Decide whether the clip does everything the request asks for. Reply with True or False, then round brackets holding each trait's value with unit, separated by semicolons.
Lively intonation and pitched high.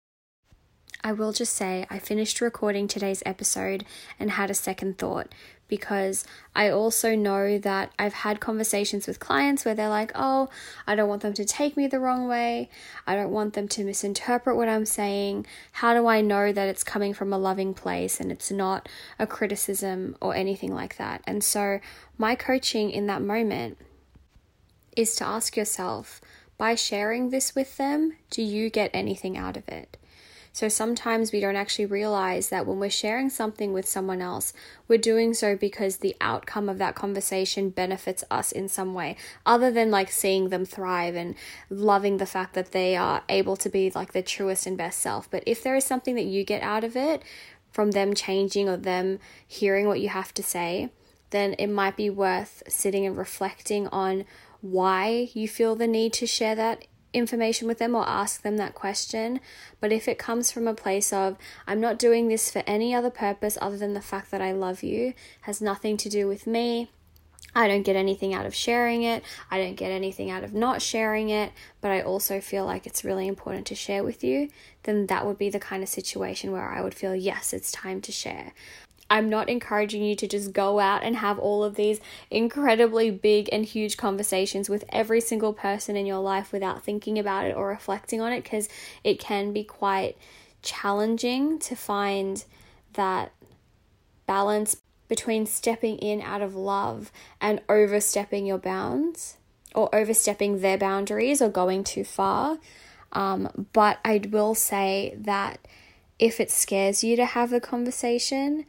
False (2.5 semitones; 205 Hz)